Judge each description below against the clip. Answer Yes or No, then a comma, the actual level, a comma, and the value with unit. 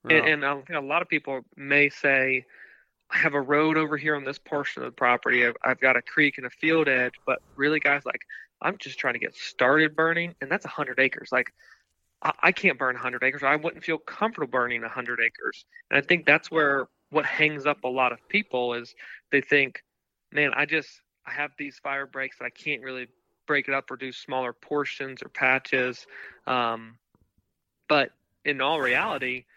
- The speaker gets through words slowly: No, fast, 205 wpm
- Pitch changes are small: No, average, 3.0 semitones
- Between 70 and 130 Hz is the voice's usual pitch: No, medium, 140 Hz